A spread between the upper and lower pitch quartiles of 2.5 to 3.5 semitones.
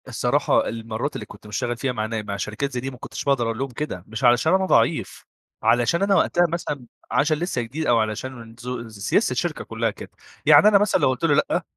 No: average, 4.9 semitones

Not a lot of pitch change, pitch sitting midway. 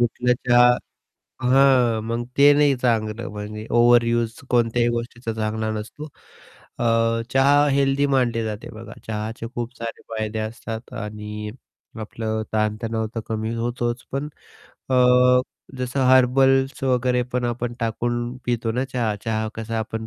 No: narrow, 2.1 semitones; low, 120 Hz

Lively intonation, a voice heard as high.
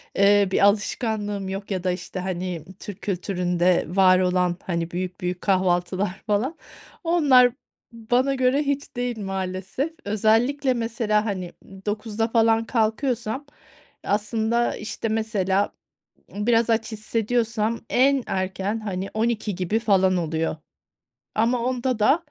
No: average, 3.8 semitones; high, 210 Hz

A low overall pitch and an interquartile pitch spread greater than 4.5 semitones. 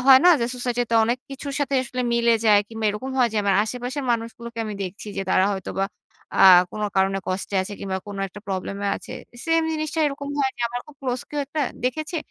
No: high, 235 Hz; average, 4.9 semitones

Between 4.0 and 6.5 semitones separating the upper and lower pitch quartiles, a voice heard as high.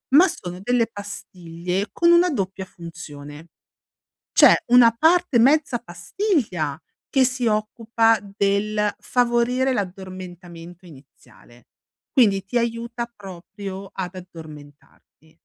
Yes: average, 5.3 semitones; high, 200 Hz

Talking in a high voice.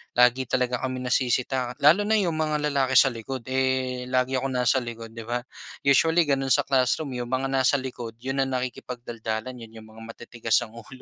No: low, 130 Hz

